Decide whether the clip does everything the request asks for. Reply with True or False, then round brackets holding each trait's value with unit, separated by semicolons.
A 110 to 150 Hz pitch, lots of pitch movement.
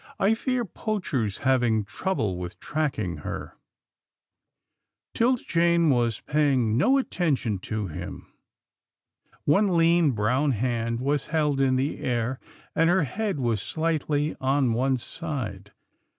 True (135 Hz; 6.2 semitones)